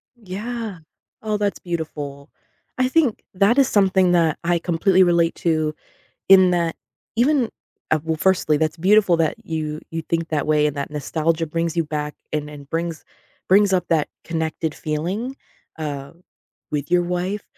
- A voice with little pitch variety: No, average, 3.6 semitones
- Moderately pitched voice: Yes, medium, 170 Hz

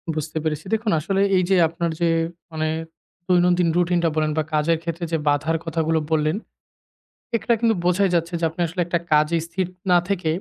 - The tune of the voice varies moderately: No, narrow, 2.1 semitones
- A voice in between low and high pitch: Yes, medium, 170 Hz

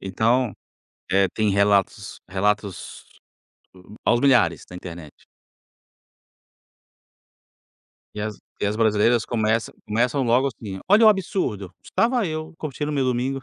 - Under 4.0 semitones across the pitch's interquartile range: No, average, 5.0 semitones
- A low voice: Yes, low, 115 Hz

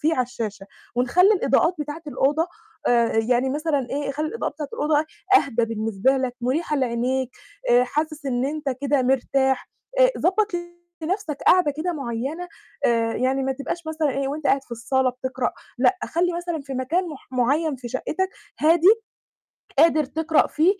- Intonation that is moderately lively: Yes, average, 3.9 semitones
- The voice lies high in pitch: Yes, very high, 280 Hz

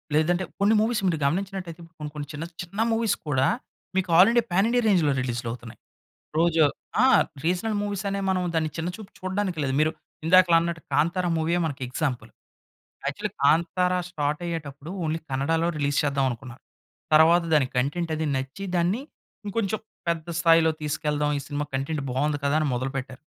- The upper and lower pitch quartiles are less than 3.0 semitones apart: No, average, 4.1 semitones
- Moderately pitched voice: Yes, medium, 165 Hz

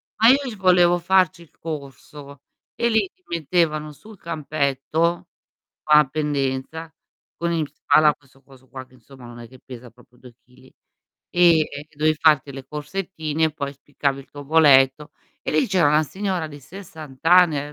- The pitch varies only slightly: No, average, 3.7 semitones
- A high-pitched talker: No, medium, 150 Hz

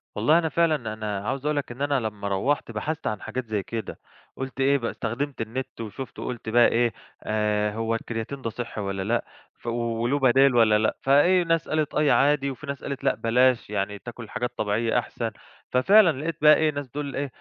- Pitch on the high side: No, low, 125 Hz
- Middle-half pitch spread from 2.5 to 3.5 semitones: No, average, 4.1 semitones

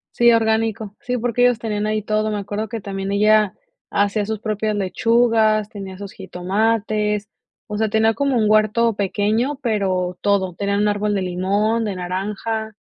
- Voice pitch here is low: No, high, 210 Hz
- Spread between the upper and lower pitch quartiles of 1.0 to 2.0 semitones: Yes, narrow, 1.7 semitones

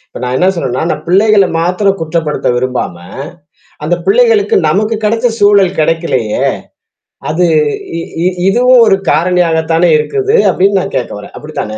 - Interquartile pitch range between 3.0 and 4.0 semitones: No, average, 4.7 semitones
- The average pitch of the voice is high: No, medium, 180 Hz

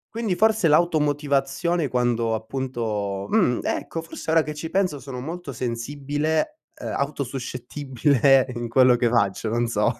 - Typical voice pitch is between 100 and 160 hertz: Yes, low, 135 Hz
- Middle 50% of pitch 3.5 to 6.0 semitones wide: Yes, average, 4.7 semitones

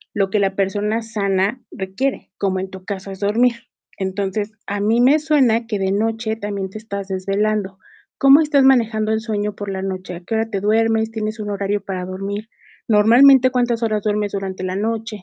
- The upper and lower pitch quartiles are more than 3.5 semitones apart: No, narrow, 2.5 semitones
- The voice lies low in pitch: No, high, 210 Hz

